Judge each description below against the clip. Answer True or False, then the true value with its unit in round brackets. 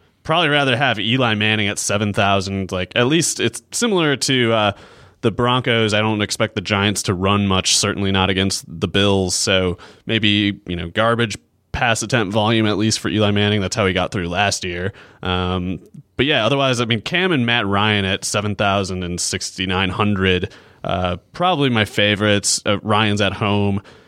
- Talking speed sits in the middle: True (180 wpm)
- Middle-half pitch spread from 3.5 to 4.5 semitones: False (2.7 semitones)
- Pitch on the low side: True (105 Hz)